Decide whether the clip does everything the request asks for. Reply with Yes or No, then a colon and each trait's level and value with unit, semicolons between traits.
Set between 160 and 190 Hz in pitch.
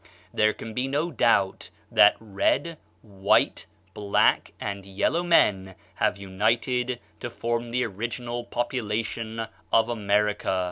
No: low, 115 Hz